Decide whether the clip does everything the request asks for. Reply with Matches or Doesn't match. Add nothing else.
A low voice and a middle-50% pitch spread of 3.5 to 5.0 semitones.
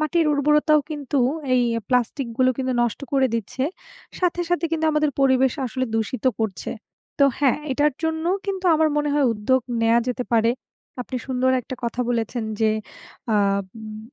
Doesn't match